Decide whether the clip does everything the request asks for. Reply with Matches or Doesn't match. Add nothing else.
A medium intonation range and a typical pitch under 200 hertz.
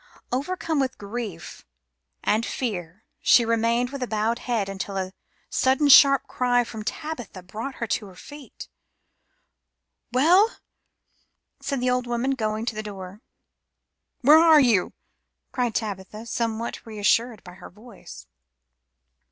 Doesn't match